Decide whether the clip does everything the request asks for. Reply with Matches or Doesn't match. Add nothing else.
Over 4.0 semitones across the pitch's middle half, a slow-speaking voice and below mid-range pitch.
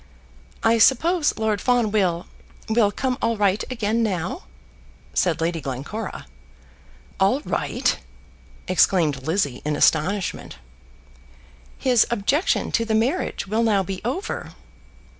Doesn't match